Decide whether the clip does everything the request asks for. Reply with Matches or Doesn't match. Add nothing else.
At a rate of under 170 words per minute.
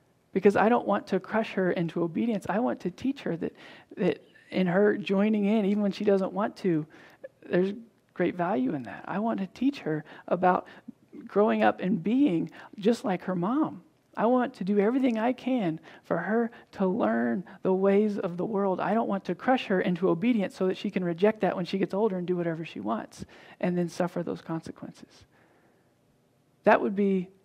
Doesn't match